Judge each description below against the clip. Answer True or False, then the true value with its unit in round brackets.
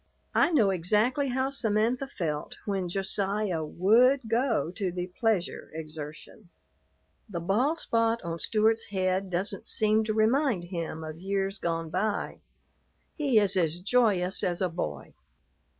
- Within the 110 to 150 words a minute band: True (140 wpm)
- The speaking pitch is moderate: False (195 Hz)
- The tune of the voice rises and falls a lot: False (4.4 semitones)